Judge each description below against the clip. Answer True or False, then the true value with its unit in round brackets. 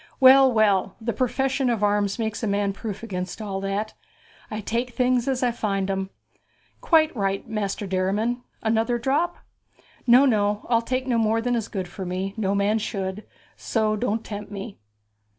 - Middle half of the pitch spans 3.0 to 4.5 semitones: True (3.4 semitones)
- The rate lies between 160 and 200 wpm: True (170 wpm)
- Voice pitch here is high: True (215 Hz)